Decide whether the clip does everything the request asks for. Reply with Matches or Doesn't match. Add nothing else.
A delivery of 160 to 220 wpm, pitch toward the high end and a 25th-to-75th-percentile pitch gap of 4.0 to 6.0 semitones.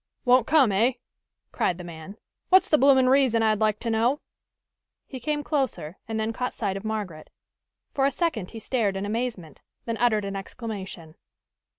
Matches